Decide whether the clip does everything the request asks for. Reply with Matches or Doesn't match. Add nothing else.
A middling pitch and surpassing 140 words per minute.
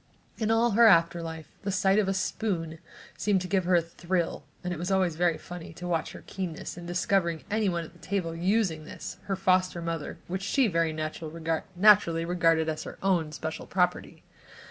Matches